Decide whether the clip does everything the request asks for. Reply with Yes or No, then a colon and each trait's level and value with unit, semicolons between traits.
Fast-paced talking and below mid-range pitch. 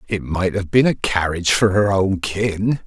Yes: fast, 210 wpm; low, 100 Hz